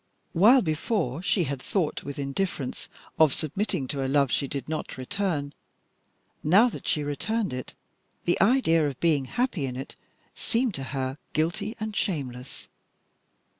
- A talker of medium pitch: Yes, medium, 155 Hz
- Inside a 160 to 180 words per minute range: No, average, 150 wpm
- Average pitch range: No, wide, 6.4 semitones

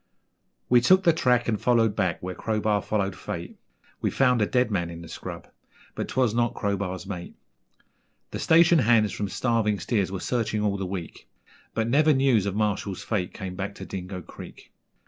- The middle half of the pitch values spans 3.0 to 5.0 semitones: Yes, average, 3.9 semitones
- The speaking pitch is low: Yes, low, 105 Hz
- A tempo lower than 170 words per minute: No, average, 185 wpm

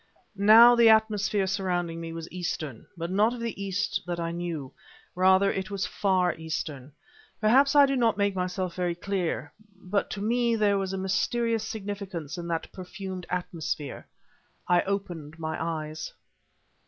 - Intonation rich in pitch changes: No, average, 3.5 semitones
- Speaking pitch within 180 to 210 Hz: Yes, high, 190 Hz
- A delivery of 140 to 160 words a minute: Yes, average, 155 wpm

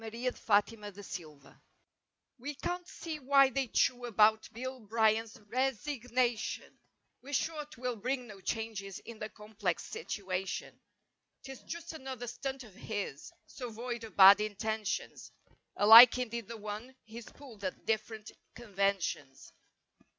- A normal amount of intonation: Yes, average, 3.5 semitones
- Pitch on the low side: No, high, 225 Hz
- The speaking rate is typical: No, slow, 130 wpm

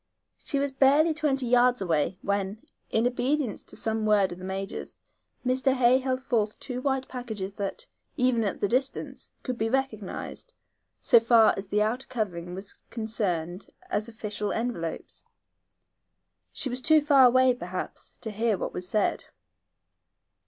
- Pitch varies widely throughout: No, average, 4.3 semitones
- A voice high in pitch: Yes, high, 230 Hz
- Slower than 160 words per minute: Yes, average, 150 wpm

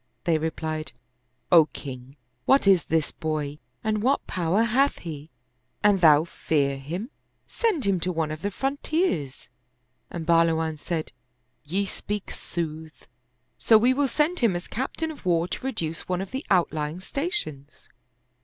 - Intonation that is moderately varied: No, wide, 5.9 semitones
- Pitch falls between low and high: Yes, medium, 170 Hz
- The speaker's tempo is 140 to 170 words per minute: Yes, average, 155 wpm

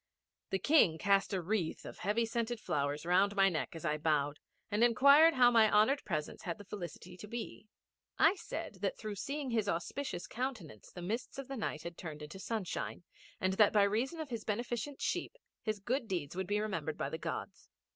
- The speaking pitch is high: Yes, high, 205 Hz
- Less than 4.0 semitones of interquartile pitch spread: No, wide, 5.5 semitones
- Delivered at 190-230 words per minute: Yes, average, 200 wpm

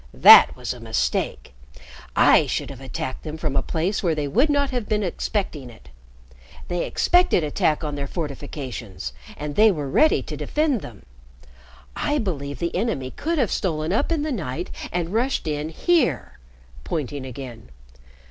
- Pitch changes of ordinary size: No, wide, 7.9 semitones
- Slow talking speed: No, average, 165 wpm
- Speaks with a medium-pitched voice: Yes, medium, 160 Hz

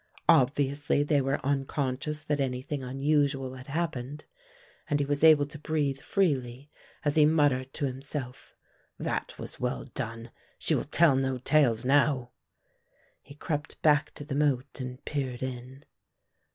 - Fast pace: No, average, 145 wpm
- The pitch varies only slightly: Yes, narrow, 2.3 semitones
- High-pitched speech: No, medium, 140 Hz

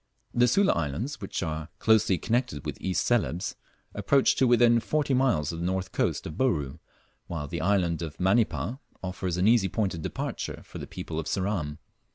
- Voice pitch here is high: No, very low, 95 Hz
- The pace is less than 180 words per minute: No, average, 185 wpm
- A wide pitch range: Yes, wide, 6.3 semitones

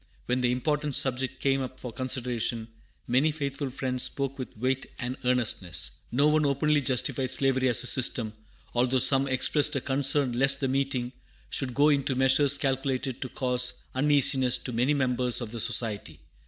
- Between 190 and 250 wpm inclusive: No, average, 170 wpm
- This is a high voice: No, low, 130 Hz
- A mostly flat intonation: Yes, narrow, 1.8 semitones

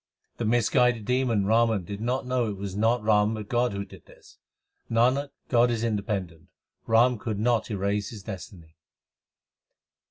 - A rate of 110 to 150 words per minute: No, average, 160 wpm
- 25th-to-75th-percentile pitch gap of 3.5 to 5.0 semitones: No, average, 3.1 semitones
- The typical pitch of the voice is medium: No, low, 110 Hz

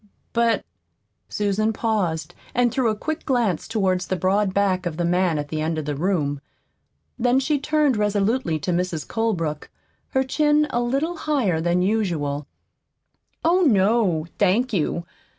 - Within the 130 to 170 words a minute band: Yes, average, 155 wpm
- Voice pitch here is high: Yes, high, 200 Hz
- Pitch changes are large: Yes, wide, 5.9 semitones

